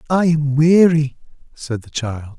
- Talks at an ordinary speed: Yes, average, 150 wpm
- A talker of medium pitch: Yes, medium, 145 Hz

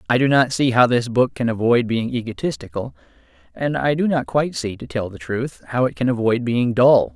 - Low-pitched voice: Yes, low, 125 Hz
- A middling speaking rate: No, fast, 225 wpm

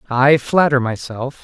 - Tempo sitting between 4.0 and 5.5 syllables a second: Yes, 4.1 syllables/s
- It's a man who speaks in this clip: Yes, male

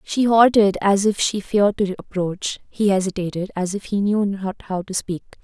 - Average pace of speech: Yes, average, 190 wpm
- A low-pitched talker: No, high, 195 Hz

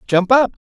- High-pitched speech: Yes, high, 220 Hz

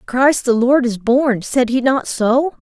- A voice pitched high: Yes, very high, 250 Hz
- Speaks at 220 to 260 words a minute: No, average, 200 wpm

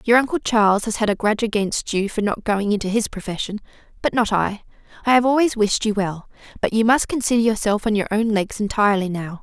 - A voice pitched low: No, high, 215 Hz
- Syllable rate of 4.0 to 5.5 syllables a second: No, 6.0 syllables/s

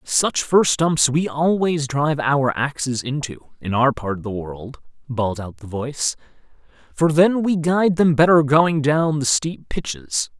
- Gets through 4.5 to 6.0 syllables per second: No, 4.3 syllables/s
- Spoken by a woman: No, male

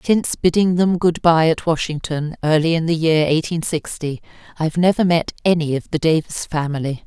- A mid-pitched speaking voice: Yes, medium, 160 Hz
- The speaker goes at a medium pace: Yes, average, 185 wpm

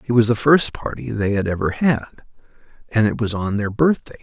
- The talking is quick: Yes, fast, 215 wpm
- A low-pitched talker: Yes, low, 115 Hz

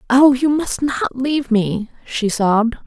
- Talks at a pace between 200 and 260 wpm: No, average, 170 wpm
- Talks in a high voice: Yes, high, 245 Hz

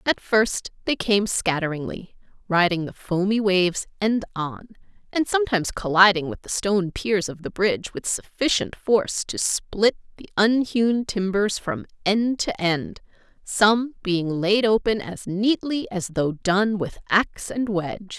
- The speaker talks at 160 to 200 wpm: No, average, 150 wpm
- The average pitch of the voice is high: Yes, high, 200 Hz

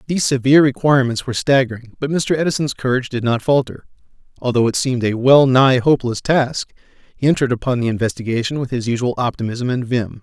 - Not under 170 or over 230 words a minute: Yes, average, 180 wpm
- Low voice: Yes, low, 125 Hz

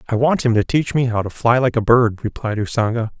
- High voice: No, low, 120 Hz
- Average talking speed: No, fast, 265 wpm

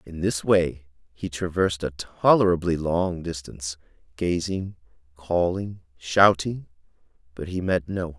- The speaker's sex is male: Yes, male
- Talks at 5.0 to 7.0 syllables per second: No, 4.5 syllables/s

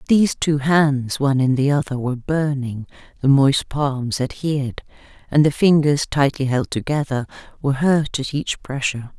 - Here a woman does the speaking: Yes, female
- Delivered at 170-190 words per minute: No, average, 155 wpm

